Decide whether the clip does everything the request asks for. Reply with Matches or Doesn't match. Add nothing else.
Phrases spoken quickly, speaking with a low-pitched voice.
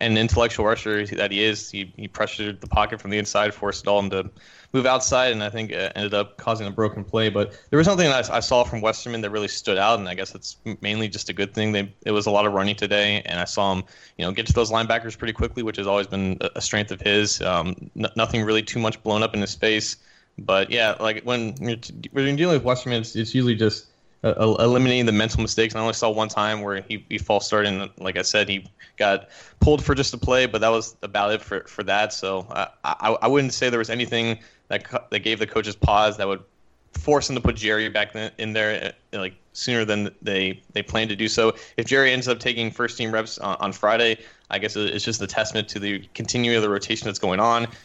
Matches